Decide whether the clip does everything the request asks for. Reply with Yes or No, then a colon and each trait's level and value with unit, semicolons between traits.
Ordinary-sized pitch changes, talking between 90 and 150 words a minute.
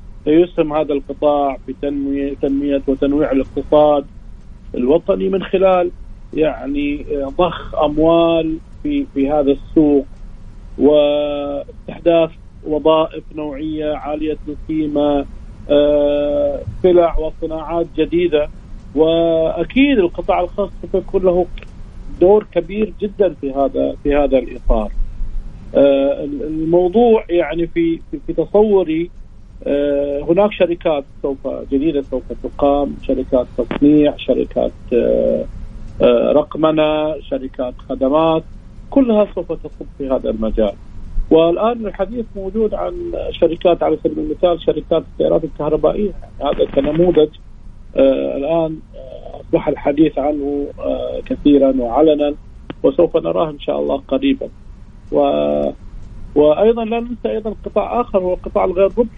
Yes: average, 4.0 semitones; average, 100 wpm